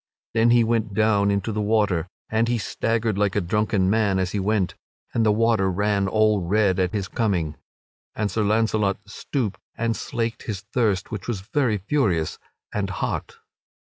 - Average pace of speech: Yes, average, 170 wpm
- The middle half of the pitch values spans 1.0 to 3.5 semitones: Yes, narrow, 2.6 semitones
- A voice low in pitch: Yes, low, 105 Hz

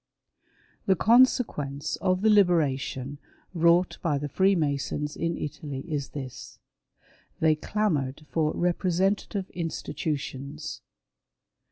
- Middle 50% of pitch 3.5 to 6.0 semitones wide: Yes, average, 4.3 semitones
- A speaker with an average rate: No, slow, 100 wpm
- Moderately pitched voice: Yes, medium, 155 Hz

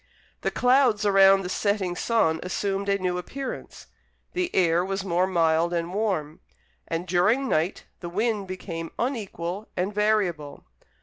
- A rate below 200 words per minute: Yes, average, 140 wpm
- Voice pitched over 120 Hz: Yes, high, 190 Hz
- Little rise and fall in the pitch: No, average, 3.4 semitones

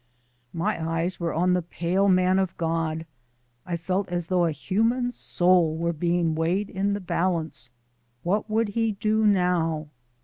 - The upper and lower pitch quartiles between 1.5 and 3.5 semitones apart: Yes, average, 3.0 semitones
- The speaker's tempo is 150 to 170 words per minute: Yes, average, 160 wpm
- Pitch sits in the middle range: Yes, medium, 180 Hz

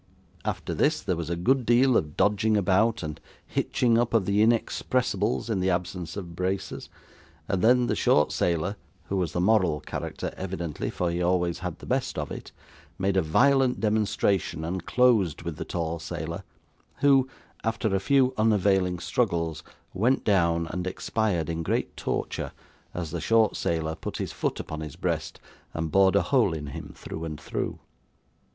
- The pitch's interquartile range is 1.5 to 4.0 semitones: No, average, 4.7 semitones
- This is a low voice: Yes, very low, 95 Hz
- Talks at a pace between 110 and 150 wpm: No, average, 170 wpm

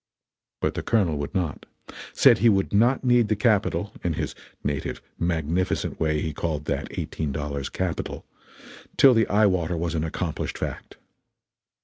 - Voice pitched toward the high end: No, very low, 85 Hz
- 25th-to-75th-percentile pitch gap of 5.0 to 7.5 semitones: Yes, average, 5.3 semitones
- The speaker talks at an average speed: Yes, average, 155 wpm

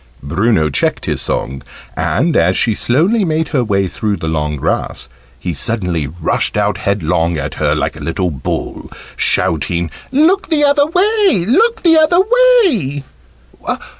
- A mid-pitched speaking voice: No, low, 120 Hz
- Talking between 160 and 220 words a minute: No, average, 150 wpm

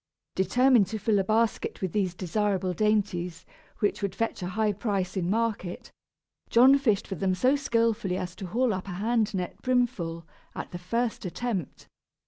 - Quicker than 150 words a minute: Yes, average, 170 wpm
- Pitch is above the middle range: Yes, high, 205 Hz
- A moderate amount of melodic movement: Yes, average, 3.9 semitones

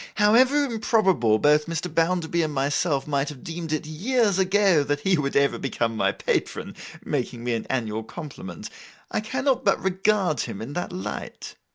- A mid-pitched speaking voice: Yes, medium, 160 Hz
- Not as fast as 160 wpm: No, average, 170 wpm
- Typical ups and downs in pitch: No, wide, 5.8 semitones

